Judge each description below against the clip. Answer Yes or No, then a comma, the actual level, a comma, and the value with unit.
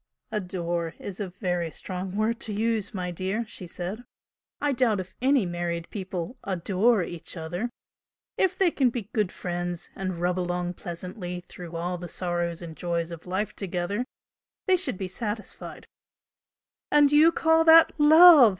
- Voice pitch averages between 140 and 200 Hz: Yes, medium, 185 Hz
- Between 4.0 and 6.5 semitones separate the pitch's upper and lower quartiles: Yes, average, 4.8 semitones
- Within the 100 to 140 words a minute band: No, average, 160 wpm